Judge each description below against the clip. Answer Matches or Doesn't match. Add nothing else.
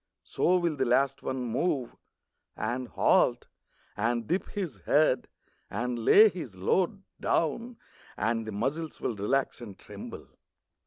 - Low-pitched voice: Matches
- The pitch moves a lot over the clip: Matches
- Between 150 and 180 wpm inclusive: Doesn't match